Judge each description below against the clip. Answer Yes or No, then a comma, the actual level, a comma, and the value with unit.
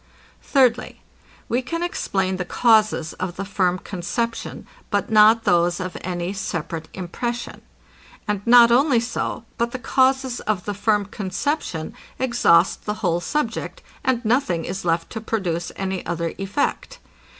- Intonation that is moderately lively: Yes, average, 4.9 semitones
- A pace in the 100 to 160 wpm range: Yes, average, 140 wpm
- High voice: Yes, high, 205 Hz